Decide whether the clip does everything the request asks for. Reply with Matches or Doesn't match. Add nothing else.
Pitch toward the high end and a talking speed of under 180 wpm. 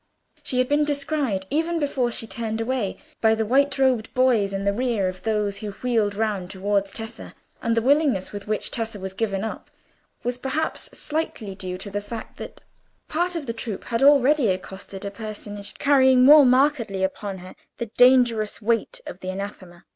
Doesn't match